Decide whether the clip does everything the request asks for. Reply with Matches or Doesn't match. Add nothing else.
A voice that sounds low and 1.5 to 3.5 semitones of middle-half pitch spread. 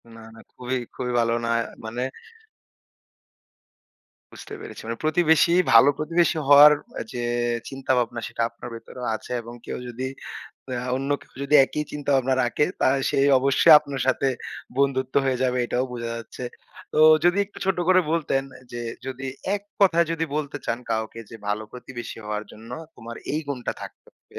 Doesn't match